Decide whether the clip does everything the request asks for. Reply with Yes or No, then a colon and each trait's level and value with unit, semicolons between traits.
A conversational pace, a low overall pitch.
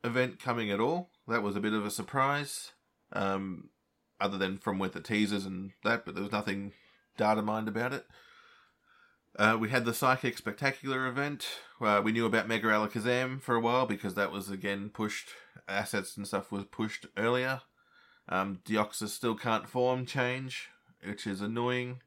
Yes: average, 175 wpm; low, 110 Hz